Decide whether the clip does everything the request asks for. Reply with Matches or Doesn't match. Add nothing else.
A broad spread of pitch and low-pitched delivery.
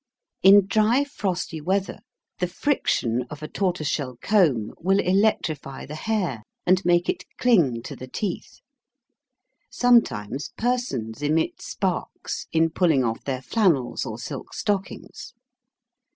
Doesn't match